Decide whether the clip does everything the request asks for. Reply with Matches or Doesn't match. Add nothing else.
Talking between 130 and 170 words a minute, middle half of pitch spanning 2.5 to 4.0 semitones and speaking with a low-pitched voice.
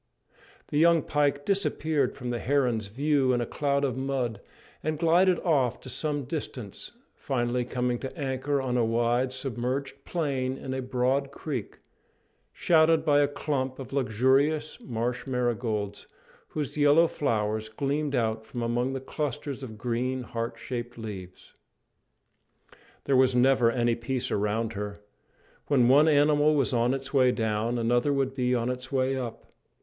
Matches